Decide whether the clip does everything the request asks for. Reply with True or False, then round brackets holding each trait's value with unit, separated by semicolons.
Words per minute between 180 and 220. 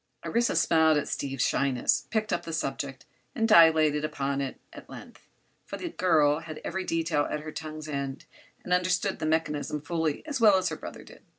True (190 wpm)